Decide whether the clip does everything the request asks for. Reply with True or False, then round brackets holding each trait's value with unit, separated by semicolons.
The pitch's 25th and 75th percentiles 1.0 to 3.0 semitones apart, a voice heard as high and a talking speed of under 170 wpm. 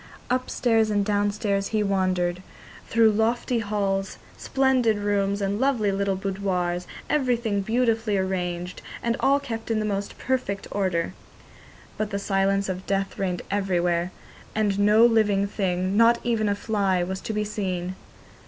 True (2.5 semitones; 200 Hz; 145 wpm)